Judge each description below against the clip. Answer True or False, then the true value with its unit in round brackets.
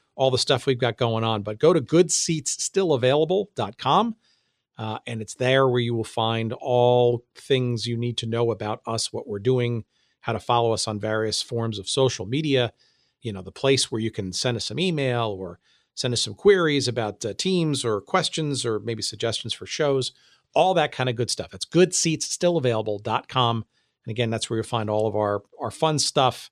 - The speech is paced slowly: False (195 wpm)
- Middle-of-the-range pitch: False (120 Hz)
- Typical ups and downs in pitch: True (3.5 semitones)